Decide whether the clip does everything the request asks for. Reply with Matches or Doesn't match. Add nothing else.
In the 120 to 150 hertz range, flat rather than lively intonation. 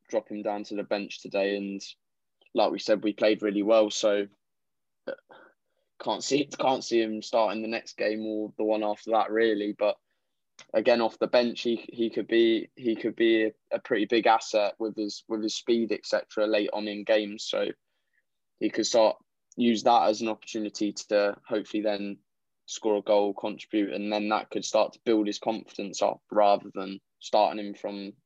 Doesn't match